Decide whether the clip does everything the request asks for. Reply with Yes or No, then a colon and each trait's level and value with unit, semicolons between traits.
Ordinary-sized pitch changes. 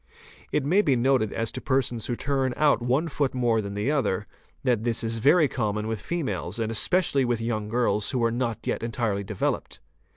Yes: average, 3.5 semitones